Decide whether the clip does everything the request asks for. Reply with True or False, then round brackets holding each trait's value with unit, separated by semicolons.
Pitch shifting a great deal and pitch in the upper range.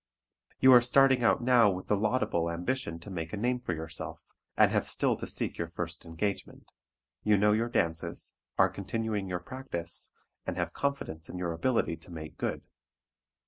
False (6.2 semitones; 100 Hz)